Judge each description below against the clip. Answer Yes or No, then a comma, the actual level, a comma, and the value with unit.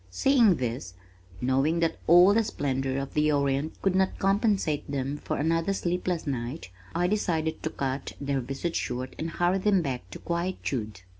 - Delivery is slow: No, average, 165 wpm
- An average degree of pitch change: Yes, average, 5.0 semitones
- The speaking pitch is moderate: Yes, medium, 155 Hz